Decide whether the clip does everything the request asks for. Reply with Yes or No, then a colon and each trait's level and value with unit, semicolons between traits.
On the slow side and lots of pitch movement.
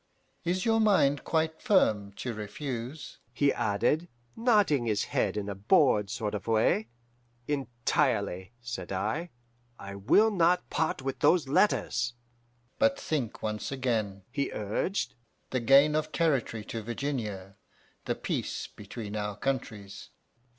Yes: slow, 130 wpm; wide, 6.7 semitones